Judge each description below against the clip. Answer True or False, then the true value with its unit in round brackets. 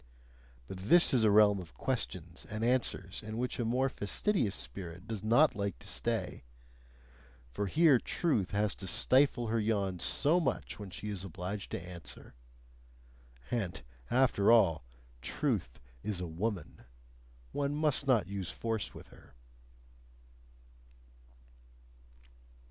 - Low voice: True (105 Hz)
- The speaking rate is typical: False (130 wpm)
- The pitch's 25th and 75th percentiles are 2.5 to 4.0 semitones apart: False (4.8 semitones)